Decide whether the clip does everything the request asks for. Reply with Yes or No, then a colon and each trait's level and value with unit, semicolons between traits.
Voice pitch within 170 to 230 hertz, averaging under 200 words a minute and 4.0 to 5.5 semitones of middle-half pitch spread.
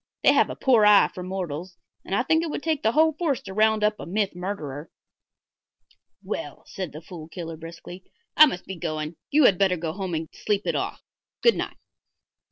No: high, 190 Hz; fast, 205 wpm; average, 4.6 semitones